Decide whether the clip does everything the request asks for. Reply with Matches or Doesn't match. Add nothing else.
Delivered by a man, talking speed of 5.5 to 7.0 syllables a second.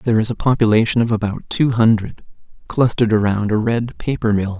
Matches